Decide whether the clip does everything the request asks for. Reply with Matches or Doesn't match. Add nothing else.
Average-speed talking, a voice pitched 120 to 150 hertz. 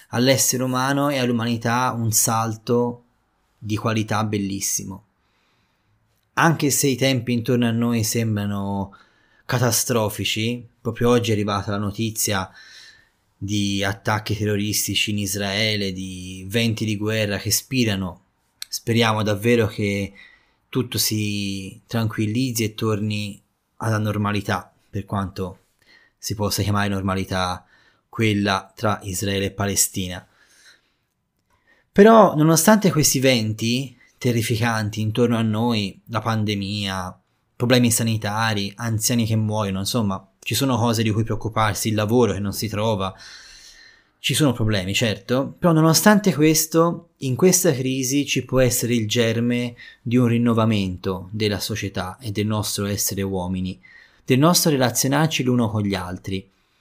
Doesn't match